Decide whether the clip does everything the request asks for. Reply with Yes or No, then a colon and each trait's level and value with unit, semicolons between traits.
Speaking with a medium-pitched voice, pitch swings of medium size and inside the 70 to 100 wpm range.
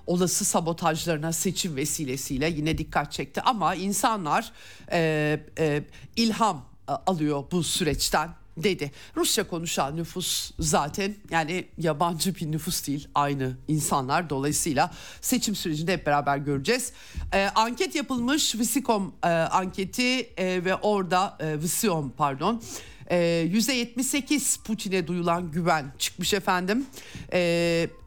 No: medium, 175 Hz; average, 4.8 semitones; average, 115 wpm